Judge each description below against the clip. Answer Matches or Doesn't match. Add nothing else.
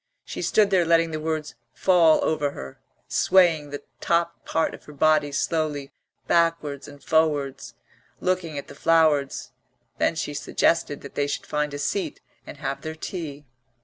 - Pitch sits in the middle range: Matches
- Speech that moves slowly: Doesn't match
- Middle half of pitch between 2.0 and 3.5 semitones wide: Matches